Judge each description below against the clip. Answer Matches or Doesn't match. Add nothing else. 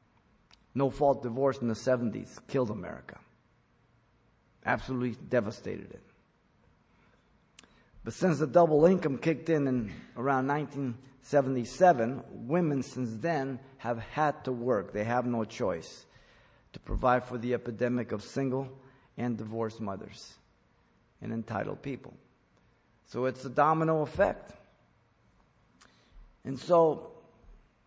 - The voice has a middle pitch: Doesn't match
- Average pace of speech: Doesn't match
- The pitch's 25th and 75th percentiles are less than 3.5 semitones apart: Matches